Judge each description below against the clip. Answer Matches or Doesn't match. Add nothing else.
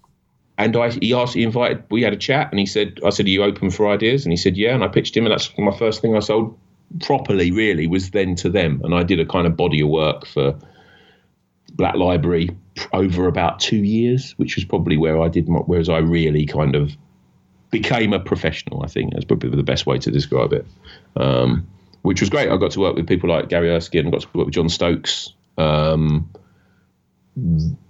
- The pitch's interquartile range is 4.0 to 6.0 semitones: Matches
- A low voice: Matches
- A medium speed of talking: Doesn't match